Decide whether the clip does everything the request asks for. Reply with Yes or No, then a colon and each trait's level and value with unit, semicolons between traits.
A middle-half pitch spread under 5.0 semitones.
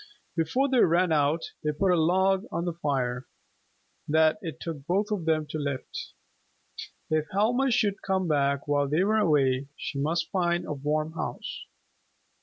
Yes: average, 4.4 semitones